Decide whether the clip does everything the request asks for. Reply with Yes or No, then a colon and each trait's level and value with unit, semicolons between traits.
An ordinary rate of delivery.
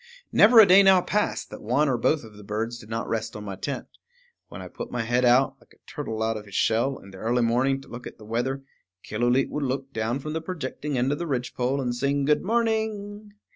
No: fast, 245 wpm